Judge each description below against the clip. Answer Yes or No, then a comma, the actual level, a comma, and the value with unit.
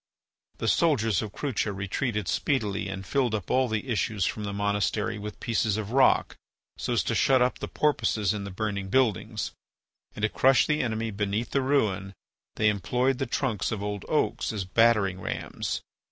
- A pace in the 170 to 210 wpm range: Yes, average, 180 wpm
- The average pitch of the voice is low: Yes, low, 110 Hz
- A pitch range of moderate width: Yes, average, 3.6 semitones